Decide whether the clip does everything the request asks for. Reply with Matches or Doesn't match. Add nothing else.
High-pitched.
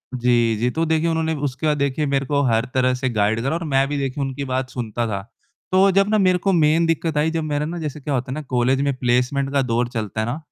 Doesn't match